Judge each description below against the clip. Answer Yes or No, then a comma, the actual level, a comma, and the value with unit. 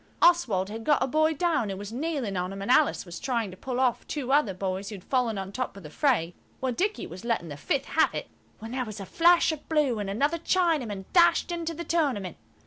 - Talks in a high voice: Yes, high, 245 Hz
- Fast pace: Yes, fast, 240 wpm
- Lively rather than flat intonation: Yes, wide, 7.8 semitones